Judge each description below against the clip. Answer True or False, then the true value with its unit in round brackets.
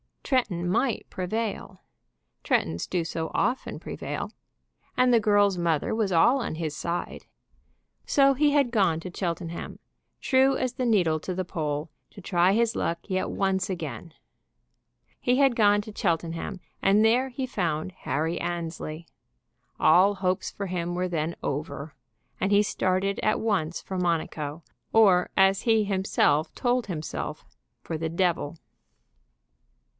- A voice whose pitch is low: False (185 Hz)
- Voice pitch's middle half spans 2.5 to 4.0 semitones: False (4.6 semitones)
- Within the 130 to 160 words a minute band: True (140 wpm)